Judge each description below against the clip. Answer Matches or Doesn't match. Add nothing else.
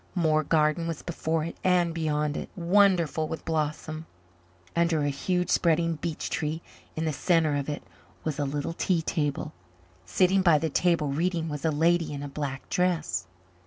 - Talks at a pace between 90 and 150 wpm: Doesn't match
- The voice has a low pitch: Doesn't match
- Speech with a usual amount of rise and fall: Doesn't match